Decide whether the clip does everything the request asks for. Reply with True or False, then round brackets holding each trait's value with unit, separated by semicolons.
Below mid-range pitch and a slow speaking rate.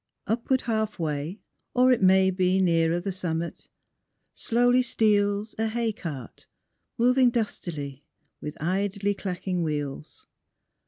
False (190 Hz; 115 wpm)